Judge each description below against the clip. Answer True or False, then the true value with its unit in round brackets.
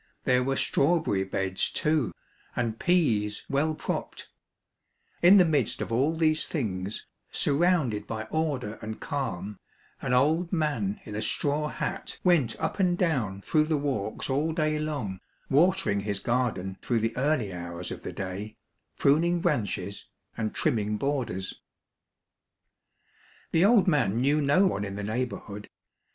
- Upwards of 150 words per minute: False (145 wpm)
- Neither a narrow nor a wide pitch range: False (6.9 semitones)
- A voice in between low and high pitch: False (130 Hz)